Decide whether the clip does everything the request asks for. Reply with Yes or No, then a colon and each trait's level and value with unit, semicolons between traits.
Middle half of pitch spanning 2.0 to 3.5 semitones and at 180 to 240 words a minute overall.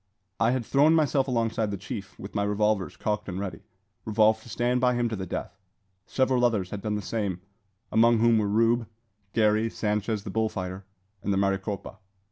Yes: narrow, 2.6 semitones; average, 190 wpm